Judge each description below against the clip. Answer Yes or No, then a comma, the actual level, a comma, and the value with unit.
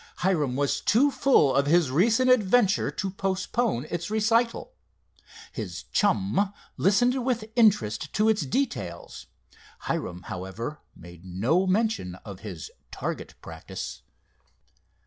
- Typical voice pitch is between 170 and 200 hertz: Yes, high, 190 Hz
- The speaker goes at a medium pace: No, slow, 115 wpm